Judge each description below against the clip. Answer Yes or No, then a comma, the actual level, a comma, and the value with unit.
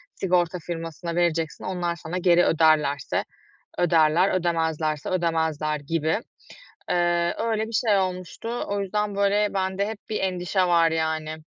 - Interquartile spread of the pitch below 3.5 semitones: Yes, average, 2.7 semitones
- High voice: No, medium, 175 Hz